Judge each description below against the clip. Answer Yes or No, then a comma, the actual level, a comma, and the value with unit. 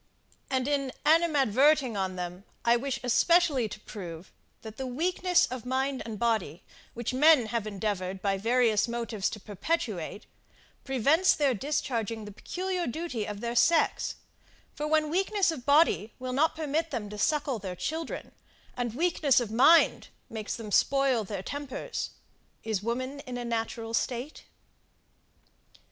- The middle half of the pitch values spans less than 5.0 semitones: No, wide, 5.4 semitones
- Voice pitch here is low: No, high, 245 Hz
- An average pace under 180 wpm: Yes, average, 145 wpm